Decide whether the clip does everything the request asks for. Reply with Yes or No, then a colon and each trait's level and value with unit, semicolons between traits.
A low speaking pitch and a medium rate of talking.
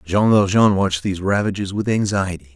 Yes: very low, 95 Hz; average, 165 wpm